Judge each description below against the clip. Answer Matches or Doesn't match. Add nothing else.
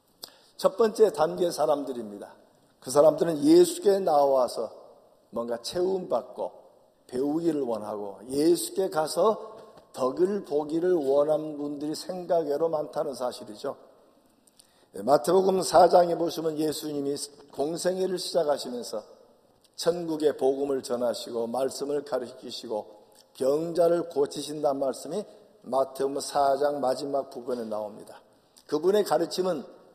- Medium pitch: Matches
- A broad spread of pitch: Doesn't match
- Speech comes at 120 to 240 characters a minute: Doesn't match